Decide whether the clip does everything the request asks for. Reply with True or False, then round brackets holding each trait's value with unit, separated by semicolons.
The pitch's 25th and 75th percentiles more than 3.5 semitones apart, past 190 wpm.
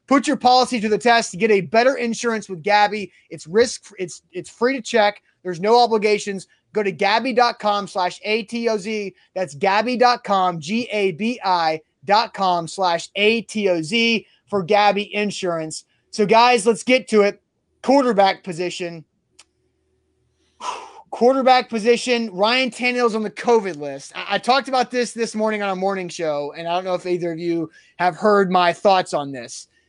False (4.4 semitones; 155 wpm)